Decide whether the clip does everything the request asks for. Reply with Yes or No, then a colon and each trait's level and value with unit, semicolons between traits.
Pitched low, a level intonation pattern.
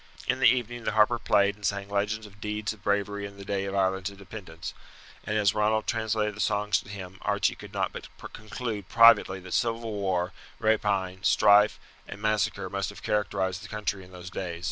Yes: low, 100 Hz; narrow, 1.8 semitones